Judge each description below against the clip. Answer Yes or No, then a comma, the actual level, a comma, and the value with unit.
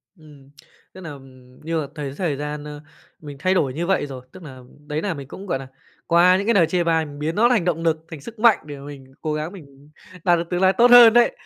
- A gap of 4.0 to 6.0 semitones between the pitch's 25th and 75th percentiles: Yes, average, 4.3 semitones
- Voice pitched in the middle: Yes, medium, 160 Hz